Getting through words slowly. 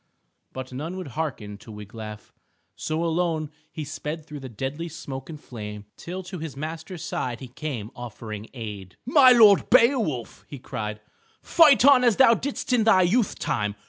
No: average, 170 wpm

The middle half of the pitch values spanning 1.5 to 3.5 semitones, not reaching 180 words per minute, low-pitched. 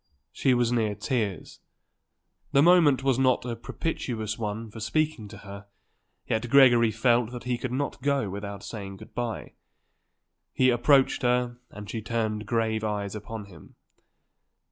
Yes: average, 2.9 semitones; average, 150 wpm; low, 115 Hz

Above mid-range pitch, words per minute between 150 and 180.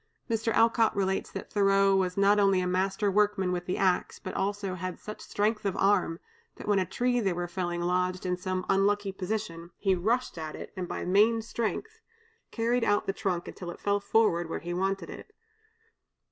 No: high, 195 Hz; average, 190 wpm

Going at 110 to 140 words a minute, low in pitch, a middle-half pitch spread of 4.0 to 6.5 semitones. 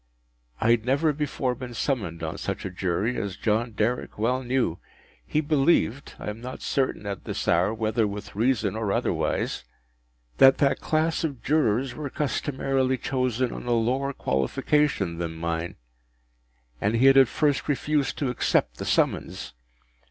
No: average, 150 wpm; low, 120 Hz; average, 5.2 semitones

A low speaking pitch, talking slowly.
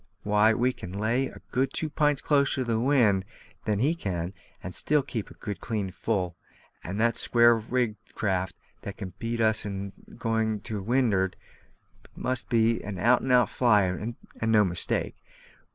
No: low, 110 Hz; average, 170 wpm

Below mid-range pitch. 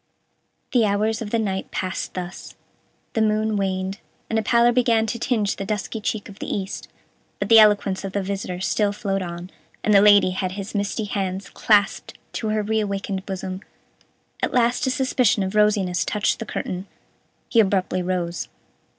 No: high, 205 Hz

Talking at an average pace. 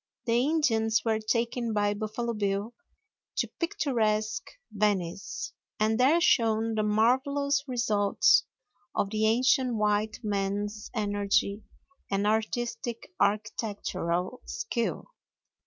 No: slow, 100 wpm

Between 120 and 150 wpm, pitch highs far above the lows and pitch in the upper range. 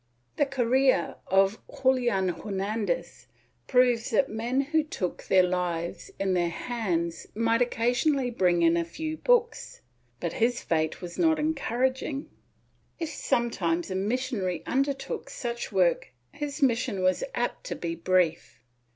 Yes: average, 140 wpm; wide, 6.5 semitones; high, 230 Hz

